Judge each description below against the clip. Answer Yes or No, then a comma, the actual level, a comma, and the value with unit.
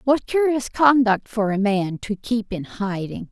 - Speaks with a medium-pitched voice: No, high, 220 Hz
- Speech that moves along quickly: No, average, 165 wpm